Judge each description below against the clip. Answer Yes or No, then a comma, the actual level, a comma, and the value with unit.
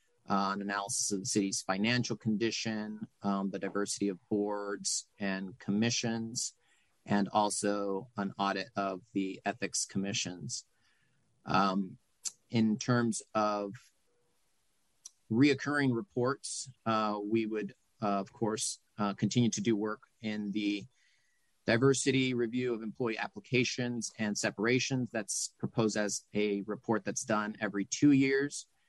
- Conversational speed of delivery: No, slow, 125 wpm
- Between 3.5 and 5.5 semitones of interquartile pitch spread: No, average, 3.0 semitones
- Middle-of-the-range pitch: No, low, 105 Hz